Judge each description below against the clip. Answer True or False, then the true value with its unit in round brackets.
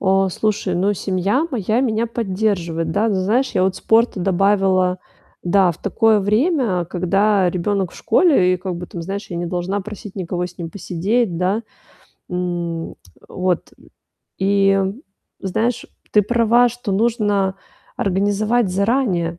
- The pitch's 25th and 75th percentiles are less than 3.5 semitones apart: True (3.1 semitones)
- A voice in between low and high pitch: False (195 Hz)